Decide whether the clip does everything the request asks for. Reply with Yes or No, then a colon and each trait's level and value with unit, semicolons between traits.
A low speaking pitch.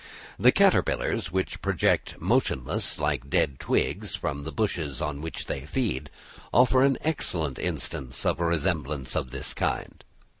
Yes: very low, 75 Hz